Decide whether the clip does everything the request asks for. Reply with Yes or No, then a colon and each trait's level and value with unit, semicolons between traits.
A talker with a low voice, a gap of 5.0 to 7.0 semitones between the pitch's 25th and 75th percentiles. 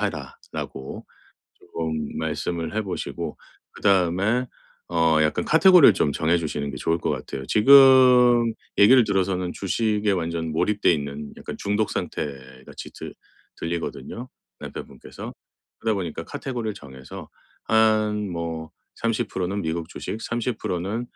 Yes: very low, 95 Hz; wide, 5.4 semitones